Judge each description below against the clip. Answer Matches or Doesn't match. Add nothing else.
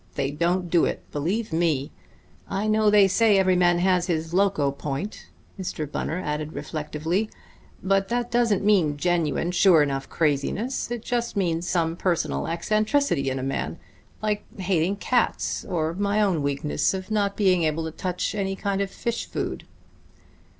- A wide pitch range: Doesn't match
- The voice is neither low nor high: Matches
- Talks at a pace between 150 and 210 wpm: Matches